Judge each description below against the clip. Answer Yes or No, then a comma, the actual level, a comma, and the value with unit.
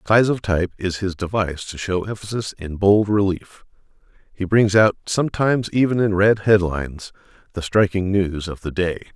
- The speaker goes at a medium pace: Yes, average, 170 wpm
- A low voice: Yes, very low, 95 Hz